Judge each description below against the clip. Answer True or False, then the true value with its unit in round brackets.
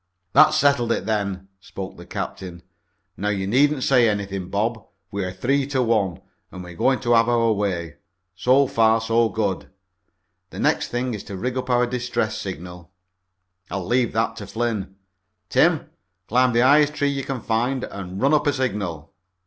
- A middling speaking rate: True (170 wpm)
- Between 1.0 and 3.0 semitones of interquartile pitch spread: False (4.6 semitones)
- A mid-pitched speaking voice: False (115 Hz)